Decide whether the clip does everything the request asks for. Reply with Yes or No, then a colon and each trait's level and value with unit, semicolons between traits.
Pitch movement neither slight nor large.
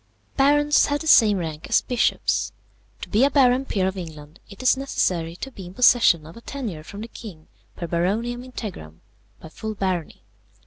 No: wide, 6.9 semitones